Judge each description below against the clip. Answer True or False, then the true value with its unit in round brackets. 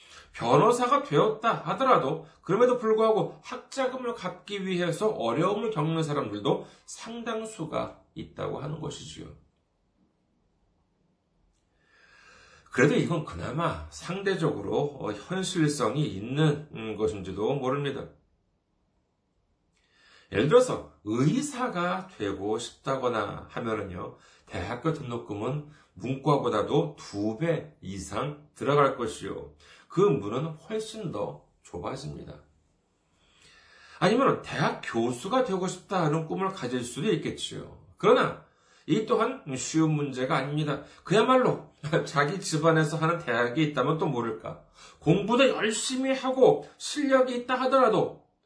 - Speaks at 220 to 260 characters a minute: True (255 characters per minute)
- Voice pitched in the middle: True (155 Hz)